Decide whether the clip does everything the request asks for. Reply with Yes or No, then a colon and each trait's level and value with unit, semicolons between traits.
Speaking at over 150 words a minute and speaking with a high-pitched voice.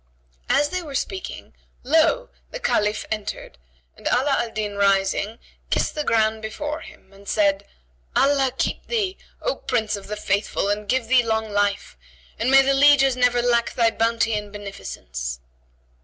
Yes: average, 160 wpm; high, 225 Hz